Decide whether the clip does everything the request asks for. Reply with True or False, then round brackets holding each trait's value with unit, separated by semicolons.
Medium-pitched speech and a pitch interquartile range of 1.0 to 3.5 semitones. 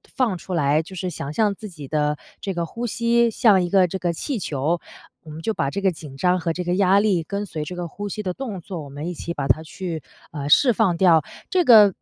False (180 Hz; 4.2 semitones)